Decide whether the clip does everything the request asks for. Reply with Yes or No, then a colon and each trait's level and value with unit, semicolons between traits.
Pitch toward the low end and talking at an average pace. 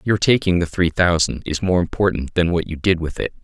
No: very low, 85 Hz; fast, 245 wpm